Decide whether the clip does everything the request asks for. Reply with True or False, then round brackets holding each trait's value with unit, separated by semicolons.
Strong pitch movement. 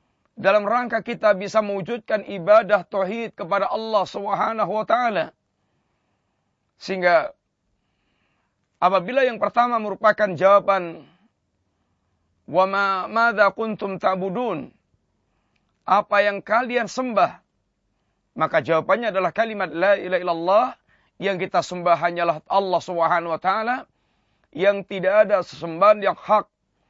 False (3.6 semitones)